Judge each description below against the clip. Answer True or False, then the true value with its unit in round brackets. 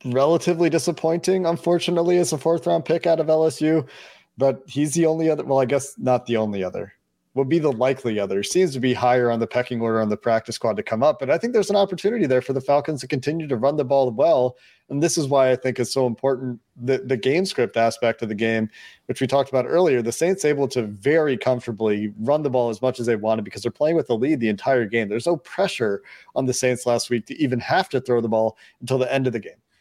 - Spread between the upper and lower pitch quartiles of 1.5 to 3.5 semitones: False (4.9 semitones)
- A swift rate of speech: True (250 wpm)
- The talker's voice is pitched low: True (130 Hz)